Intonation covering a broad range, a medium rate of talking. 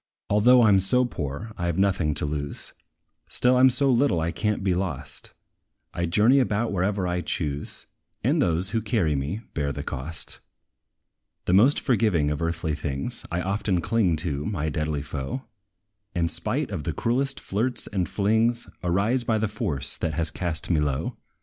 Yes: wide, 5.9 semitones; average, 175 wpm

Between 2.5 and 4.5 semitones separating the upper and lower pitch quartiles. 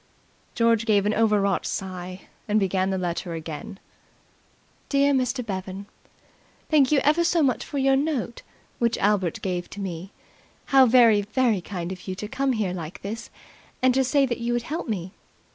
No: wide, 5.4 semitones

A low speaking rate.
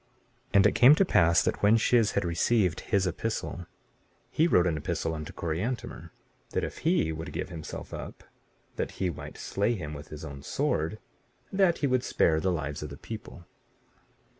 No: average, 185 wpm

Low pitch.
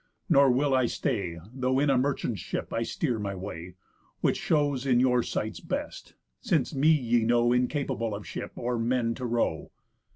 Yes: low, 125 Hz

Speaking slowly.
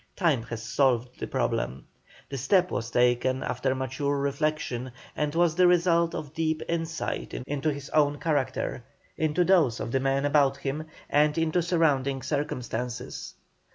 No: average, 150 wpm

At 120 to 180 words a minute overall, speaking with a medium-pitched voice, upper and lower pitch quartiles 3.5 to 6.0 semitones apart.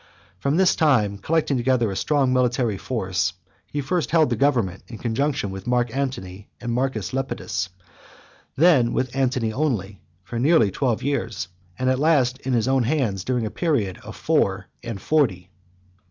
No: average, 165 wpm; low, 125 Hz; average, 4.3 semitones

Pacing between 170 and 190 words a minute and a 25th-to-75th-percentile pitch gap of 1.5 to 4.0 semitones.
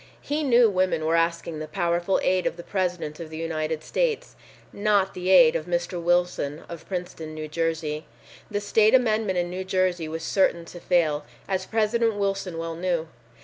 Yes: average, 180 wpm; average, 3.0 semitones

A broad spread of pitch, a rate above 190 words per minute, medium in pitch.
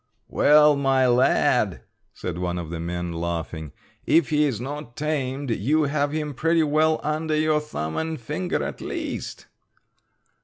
No: wide, 8.7 semitones; average, 150 wpm; medium, 145 Hz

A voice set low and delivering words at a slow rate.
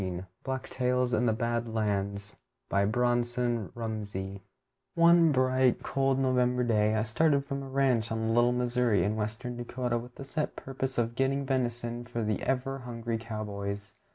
No: low, 120 Hz; average, 155 wpm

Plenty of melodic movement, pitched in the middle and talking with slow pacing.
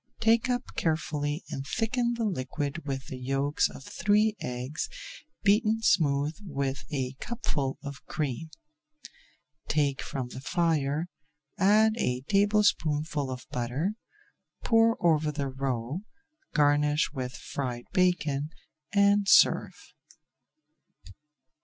Yes: wide, 6.7 semitones; medium, 150 Hz; slow, 110 wpm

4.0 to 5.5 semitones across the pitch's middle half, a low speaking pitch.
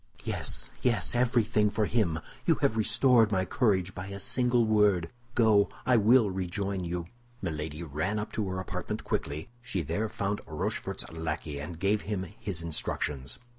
Yes: average, 4.3 semitones; low, 100 Hz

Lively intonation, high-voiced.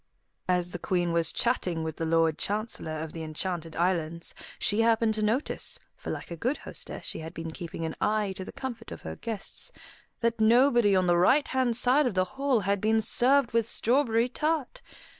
Yes: wide, 5.9 semitones; high, 210 Hz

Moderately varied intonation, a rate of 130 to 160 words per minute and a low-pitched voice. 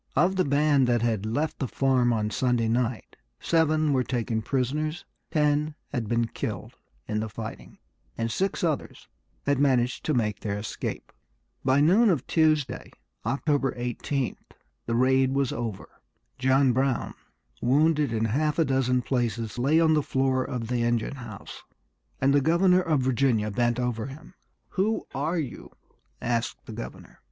Yes: average, 4.1 semitones; average, 155 wpm; low, 130 Hz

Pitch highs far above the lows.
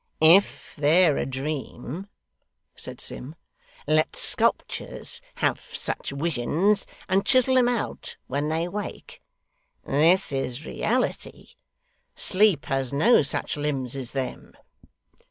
Yes: wide, 6.0 semitones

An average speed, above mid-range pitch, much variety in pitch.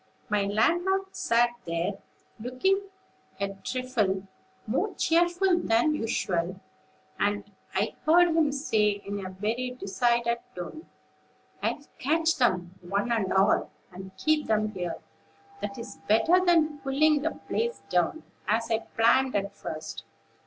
No: slow, 130 wpm; high, 235 Hz; wide, 7.6 semitones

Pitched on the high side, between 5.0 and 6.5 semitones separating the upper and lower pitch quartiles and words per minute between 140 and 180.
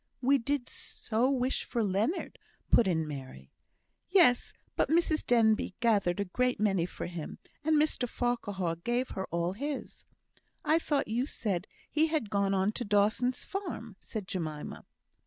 Yes: high, 225 Hz; wide, 5.5 semitones; average, 155 wpm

